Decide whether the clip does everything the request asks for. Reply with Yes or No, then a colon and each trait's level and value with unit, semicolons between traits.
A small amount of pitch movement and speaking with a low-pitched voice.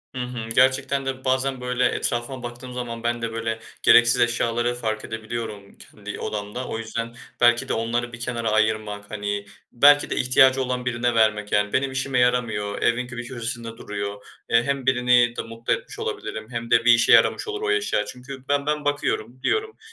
Yes: narrow, 2.2 semitones; low, 120 Hz